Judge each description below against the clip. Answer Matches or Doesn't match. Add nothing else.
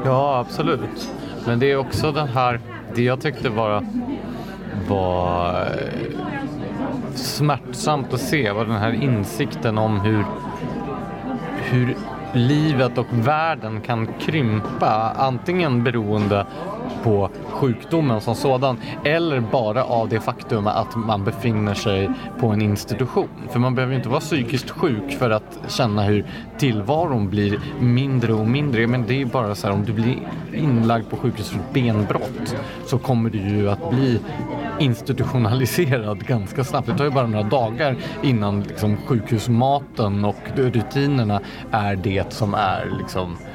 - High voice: Doesn't match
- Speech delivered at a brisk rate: Doesn't match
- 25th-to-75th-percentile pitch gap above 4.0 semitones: Doesn't match